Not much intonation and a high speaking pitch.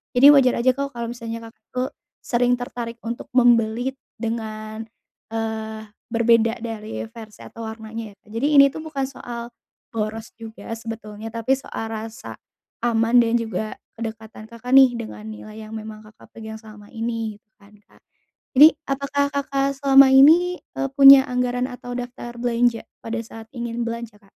Yes: narrow, 2.2 semitones; high, 230 Hz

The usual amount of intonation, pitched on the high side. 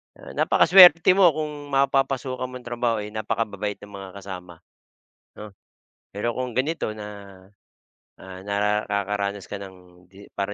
No: average, 4.4 semitones; low, 105 Hz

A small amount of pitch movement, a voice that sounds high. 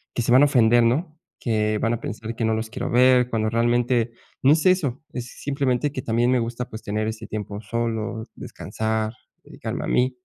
No: narrow, 2.3 semitones; low, 115 Hz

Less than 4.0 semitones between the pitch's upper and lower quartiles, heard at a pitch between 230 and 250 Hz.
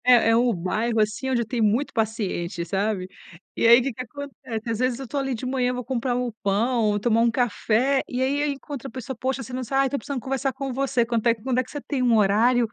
Yes: average, 2.8 semitones; high, 245 Hz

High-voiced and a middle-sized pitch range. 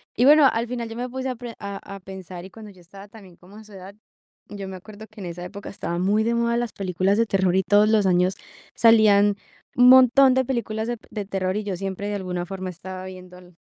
Yes: high, 200 Hz; average, 3.4 semitones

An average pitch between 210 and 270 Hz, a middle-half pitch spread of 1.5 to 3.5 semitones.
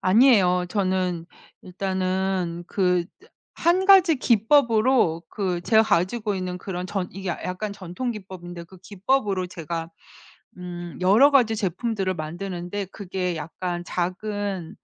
No: medium, 185 Hz; average, 3.1 semitones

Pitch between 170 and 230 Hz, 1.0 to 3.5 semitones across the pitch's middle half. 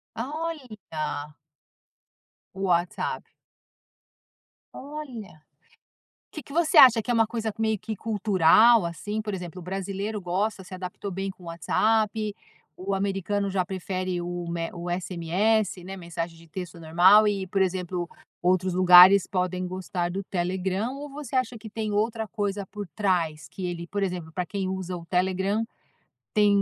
Yes: high, 190 Hz; average, 3.2 semitones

